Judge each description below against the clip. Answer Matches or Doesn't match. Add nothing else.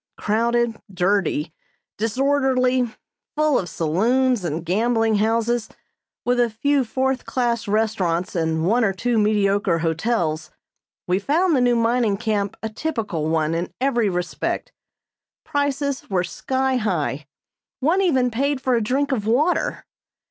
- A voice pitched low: Doesn't match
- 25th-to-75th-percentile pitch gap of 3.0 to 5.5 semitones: Matches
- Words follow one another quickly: Doesn't match